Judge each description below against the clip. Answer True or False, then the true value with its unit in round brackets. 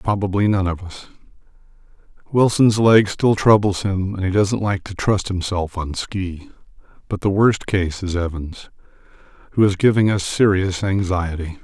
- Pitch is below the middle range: True (95 Hz)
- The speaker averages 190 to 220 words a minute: False (155 wpm)